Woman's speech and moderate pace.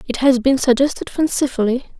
Yes: female; average, 150 wpm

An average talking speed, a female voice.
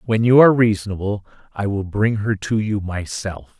No: average, 185 wpm; male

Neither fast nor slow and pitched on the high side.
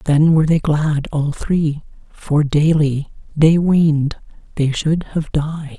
No: average, 145 wpm; medium, 150 Hz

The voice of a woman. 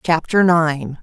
Yes: female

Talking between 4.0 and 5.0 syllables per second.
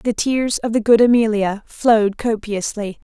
Yes: 4.5 syllables/s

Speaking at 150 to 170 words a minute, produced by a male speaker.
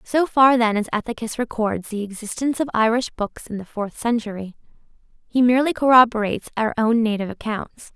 No: average, 165 wpm; female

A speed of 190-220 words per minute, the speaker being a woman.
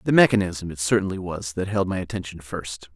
No: fast, 205 wpm; male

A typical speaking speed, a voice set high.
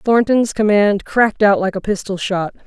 Yes: average, 180 wpm; high, 205 Hz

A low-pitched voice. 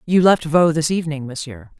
No: medium, 155 Hz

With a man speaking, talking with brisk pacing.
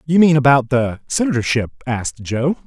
No: male; average, 160 wpm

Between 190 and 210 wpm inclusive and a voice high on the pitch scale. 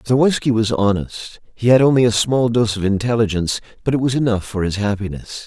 No: average, 200 wpm; low, 110 Hz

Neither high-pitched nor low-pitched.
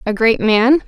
No: high, 235 Hz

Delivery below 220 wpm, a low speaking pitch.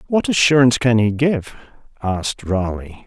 Yes: slow, 135 wpm; low, 120 Hz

